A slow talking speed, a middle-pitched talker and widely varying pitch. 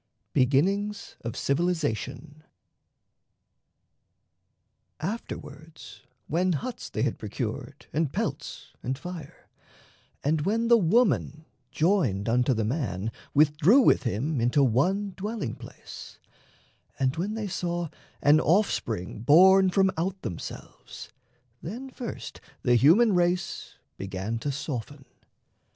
Yes: slow, 110 wpm; medium, 155 Hz; wide, 6.7 semitones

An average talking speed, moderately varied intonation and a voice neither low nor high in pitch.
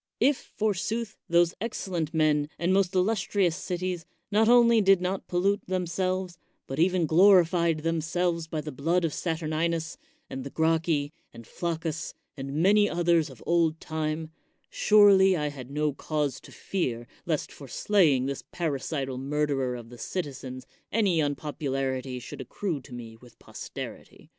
Yes: average, 150 wpm; average, 4.2 semitones; medium, 165 Hz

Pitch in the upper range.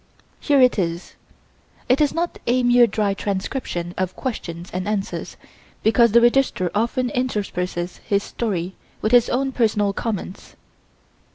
Yes: high, 215 Hz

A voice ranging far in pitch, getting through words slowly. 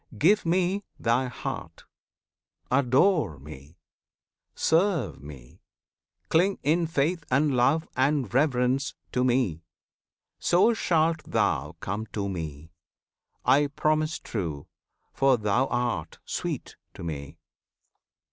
Yes: wide, 8.1 semitones; slow, 105 wpm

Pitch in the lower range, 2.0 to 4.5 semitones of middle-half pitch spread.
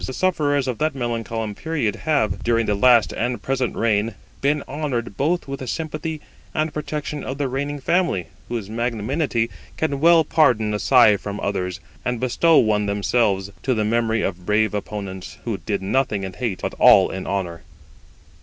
No: low, 120 Hz; wide, 5.5 semitones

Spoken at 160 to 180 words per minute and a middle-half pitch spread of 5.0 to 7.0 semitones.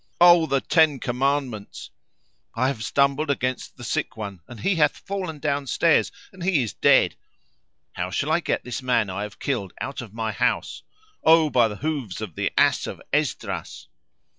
Yes: average, 175 wpm; wide, 5.5 semitones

